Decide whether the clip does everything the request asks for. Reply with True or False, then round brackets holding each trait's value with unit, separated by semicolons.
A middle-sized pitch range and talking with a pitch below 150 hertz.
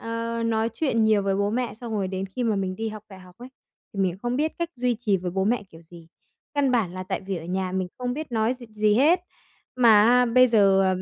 False (4.1 semitones; 220 Hz)